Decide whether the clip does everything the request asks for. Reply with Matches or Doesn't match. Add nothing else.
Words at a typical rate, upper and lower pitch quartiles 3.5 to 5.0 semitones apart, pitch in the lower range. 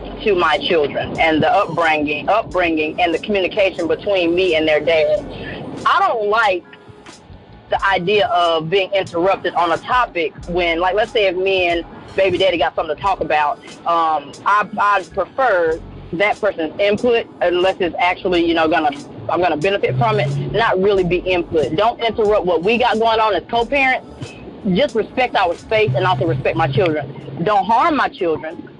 Doesn't match